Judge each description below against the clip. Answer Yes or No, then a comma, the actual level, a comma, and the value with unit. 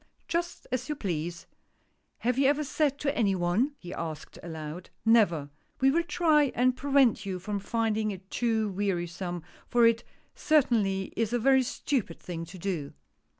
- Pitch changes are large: Yes, wide, 6.9 semitones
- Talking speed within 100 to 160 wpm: No, average, 170 wpm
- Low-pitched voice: No, high, 220 Hz